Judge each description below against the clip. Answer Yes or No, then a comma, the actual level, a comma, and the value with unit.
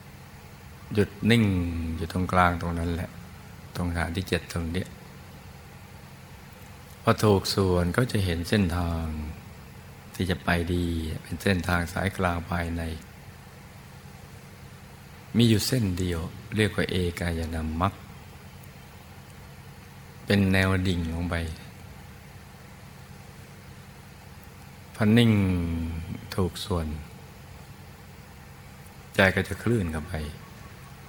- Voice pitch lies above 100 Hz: No, very low, 90 Hz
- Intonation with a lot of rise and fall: No, average, 2.9 semitones